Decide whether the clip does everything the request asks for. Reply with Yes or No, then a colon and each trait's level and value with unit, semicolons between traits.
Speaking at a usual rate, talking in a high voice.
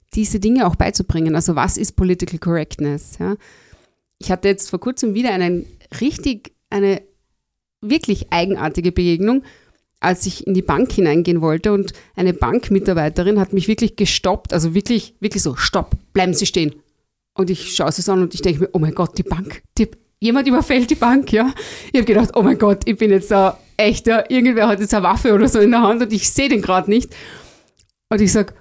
No: fast, 195 wpm; high, 200 Hz